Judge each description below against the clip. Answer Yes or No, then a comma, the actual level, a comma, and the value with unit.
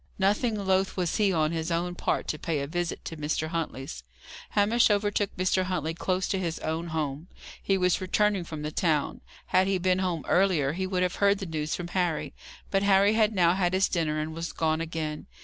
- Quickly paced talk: Yes, fast, 210 wpm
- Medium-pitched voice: Yes, medium, 175 Hz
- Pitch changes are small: No, average, 3.2 semitones